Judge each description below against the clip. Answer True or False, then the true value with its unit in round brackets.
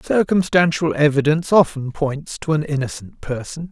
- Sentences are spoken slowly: True (130 wpm)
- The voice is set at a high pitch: False (150 Hz)